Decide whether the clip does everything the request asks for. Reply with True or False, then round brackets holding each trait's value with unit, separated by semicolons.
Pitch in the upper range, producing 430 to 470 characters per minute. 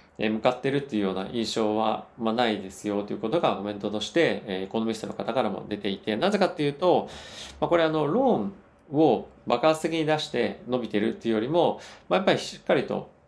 False (115 Hz; 440 characters per minute)